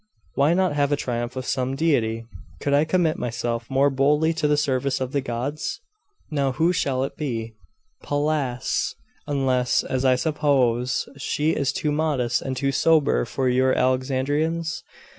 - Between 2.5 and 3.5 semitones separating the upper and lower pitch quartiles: Yes, average, 2.8 semitones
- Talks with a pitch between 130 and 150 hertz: Yes, low, 135 Hz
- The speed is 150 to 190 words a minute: Yes, average, 160 wpm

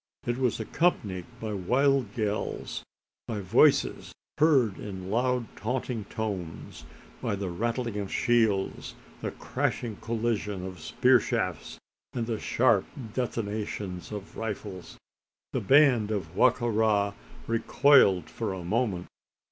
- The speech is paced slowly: Yes, slow, 125 wpm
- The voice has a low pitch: Yes, low, 110 Hz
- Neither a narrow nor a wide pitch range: Yes, average, 3.5 semitones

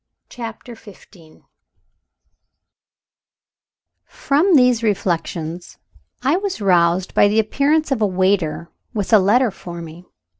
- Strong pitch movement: Yes, wide, 6.0 semitones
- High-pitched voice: Yes, high, 205 Hz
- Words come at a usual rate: No, slow, 110 wpm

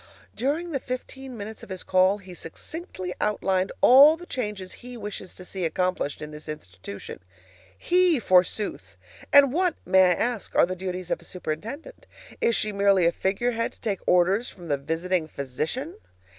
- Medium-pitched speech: No, high, 195 Hz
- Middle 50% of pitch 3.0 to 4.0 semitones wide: No, wide, 5.6 semitones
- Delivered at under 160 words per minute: No, average, 170 wpm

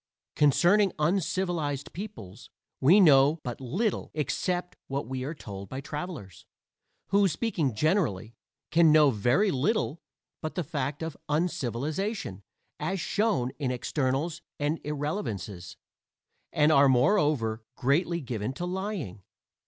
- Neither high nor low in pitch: Yes, medium, 150 Hz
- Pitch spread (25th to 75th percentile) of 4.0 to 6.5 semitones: Yes, wide, 5.6 semitones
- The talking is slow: Yes, slow, 120 wpm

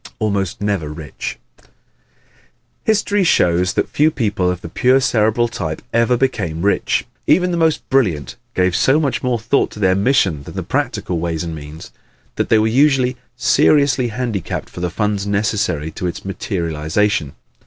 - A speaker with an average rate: Yes, average, 165 wpm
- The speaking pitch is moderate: No, low, 105 Hz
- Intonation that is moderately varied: No, wide, 6.7 semitones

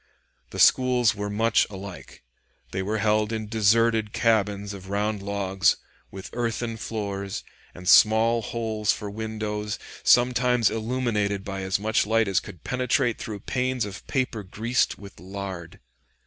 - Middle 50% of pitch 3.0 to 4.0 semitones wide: No, narrow, 2.4 semitones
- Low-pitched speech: Yes, low, 105 Hz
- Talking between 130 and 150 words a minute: Yes, average, 140 wpm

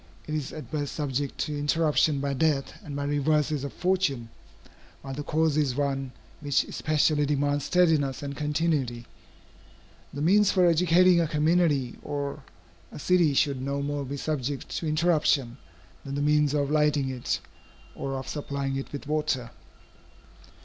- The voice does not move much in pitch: Yes, narrow, 1.9 semitones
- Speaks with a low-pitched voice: No, medium, 145 Hz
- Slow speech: No, average, 155 wpm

